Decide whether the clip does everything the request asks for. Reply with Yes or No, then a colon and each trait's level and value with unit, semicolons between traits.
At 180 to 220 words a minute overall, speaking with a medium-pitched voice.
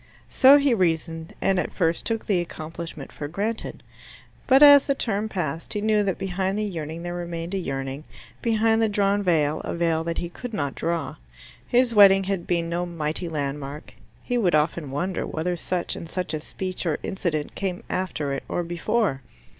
Yes: average, 185 wpm; medium, 175 Hz